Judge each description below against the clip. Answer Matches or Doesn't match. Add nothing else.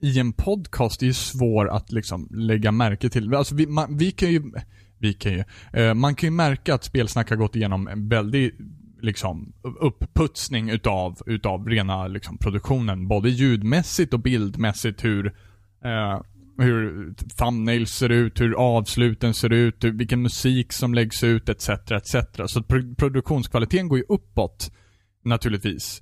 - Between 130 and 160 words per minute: Matches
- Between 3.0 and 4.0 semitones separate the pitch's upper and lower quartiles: Matches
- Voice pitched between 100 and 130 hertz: Matches